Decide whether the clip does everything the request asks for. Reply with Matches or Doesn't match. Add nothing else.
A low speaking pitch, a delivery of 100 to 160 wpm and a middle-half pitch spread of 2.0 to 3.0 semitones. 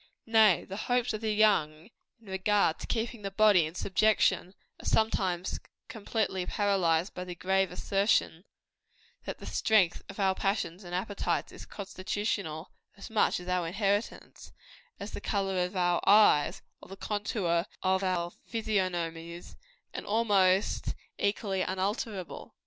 Doesn't match